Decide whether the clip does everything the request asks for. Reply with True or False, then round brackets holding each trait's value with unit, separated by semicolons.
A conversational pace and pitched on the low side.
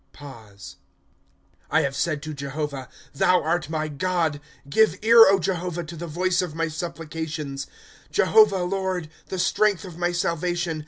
False (155 wpm; 165 Hz)